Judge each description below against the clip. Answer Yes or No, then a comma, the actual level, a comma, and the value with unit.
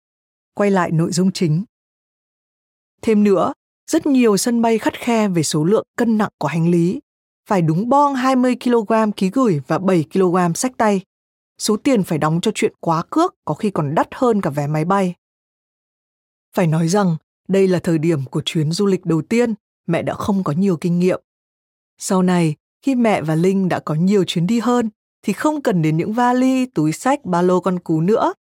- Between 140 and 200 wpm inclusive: Yes, average, 195 wpm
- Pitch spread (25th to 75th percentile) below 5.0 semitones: No, wide, 5.4 semitones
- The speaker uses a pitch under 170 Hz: No, high, 190 Hz